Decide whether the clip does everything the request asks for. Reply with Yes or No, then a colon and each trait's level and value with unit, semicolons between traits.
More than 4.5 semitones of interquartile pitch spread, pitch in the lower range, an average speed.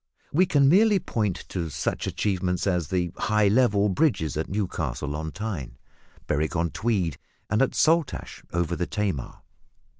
Yes: wide, 5.5 semitones; very low, 95 Hz; average, 150 wpm